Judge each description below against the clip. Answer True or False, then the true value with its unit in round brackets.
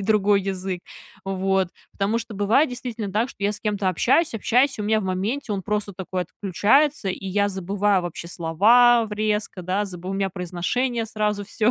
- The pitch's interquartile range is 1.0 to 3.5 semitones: True (2.8 semitones)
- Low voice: False (205 Hz)